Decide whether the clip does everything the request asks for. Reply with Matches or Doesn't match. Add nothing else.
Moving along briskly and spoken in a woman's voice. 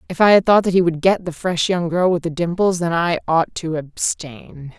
Matches